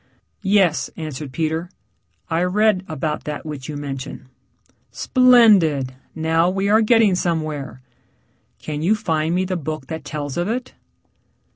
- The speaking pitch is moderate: Yes, medium, 160 Hz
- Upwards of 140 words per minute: No, slow, 135 wpm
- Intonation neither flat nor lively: Yes, average, 4.3 semitones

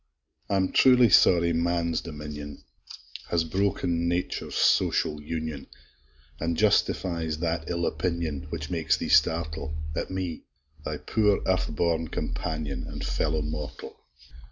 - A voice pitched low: Yes, very low, 85 Hz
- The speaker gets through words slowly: Yes, slow, 120 wpm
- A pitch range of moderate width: No, narrow, 2.2 semitones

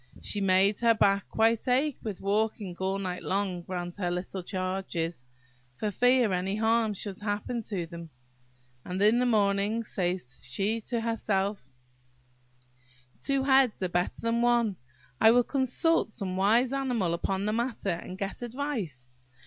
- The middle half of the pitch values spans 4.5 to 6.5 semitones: No, average, 3.9 semitones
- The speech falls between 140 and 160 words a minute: Yes, average, 150 wpm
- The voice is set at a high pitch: Yes, high, 205 Hz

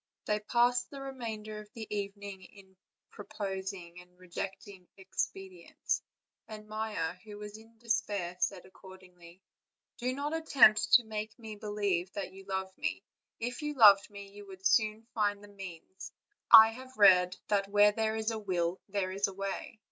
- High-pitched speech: Yes, high, 205 Hz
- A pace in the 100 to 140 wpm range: No, average, 165 wpm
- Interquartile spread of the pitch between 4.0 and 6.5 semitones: No, narrow, 2.4 semitones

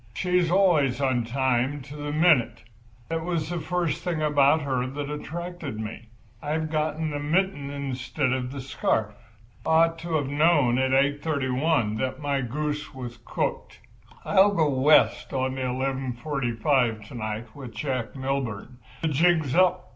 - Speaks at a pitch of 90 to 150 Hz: Yes, medium, 140 Hz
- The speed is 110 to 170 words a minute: Yes, average, 155 wpm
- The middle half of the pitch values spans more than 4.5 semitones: No, average, 3.6 semitones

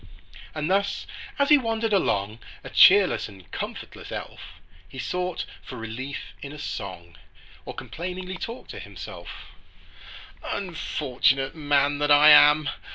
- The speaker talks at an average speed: No, slow, 130 wpm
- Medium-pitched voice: Yes, medium, 150 Hz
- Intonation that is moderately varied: No, wide, 5.9 semitones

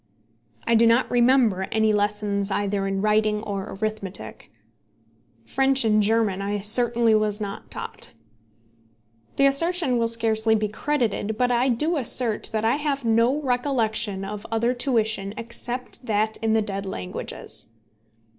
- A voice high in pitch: Yes, high, 220 Hz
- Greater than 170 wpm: No, average, 140 wpm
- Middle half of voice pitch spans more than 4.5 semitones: No, average, 2.8 semitones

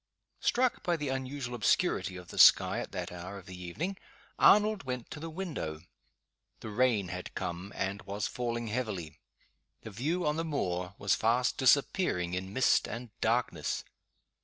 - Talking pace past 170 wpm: No, average, 160 wpm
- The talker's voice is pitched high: No, low, 120 Hz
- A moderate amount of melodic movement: No, wide, 7.6 semitones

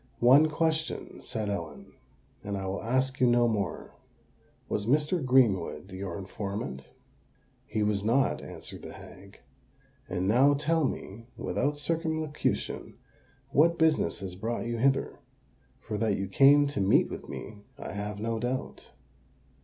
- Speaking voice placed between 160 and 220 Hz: No, low, 115 Hz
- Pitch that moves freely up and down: Yes, wide, 6.2 semitones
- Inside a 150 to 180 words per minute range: No, slow, 135 wpm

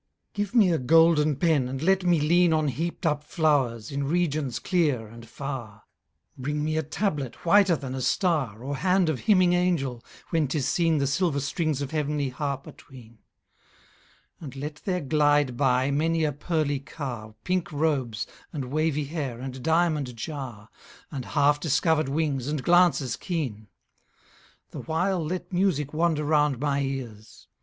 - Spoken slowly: No, average, 160 wpm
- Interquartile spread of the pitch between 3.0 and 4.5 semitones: Yes, average, 3.7 semitones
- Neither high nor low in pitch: Yes, medium, 150 Hz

